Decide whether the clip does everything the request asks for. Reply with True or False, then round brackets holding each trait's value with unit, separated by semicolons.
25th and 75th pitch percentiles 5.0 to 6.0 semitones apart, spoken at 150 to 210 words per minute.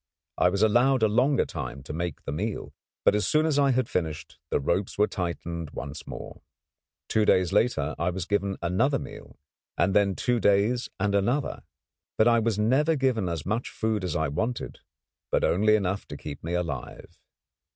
True (5.4 semitones; 185 wpm)